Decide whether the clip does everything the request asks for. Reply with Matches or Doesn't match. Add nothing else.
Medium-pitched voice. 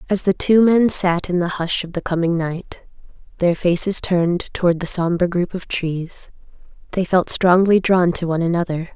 Matches